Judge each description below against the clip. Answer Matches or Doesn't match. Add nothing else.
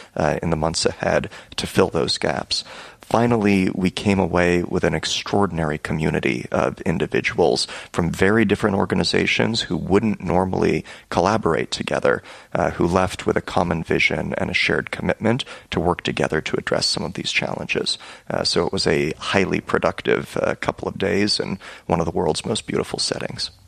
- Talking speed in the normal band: Matches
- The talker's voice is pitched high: Doesn't match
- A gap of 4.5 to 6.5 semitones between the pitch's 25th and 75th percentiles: Doesn't match